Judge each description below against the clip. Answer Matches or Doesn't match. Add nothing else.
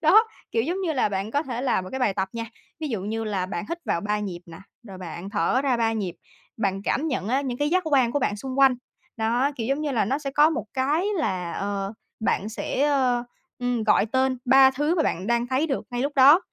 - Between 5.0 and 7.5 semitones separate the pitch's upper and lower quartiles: Matches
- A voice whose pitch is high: Matches